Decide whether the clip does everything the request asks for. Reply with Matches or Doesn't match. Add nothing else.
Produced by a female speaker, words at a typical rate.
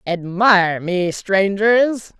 Doesn't match